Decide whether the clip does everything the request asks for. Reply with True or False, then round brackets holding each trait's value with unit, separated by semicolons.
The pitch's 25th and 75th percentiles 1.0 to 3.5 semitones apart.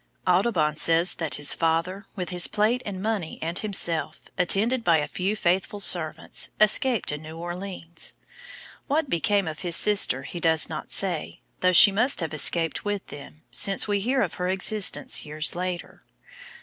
False (3.9 semitones)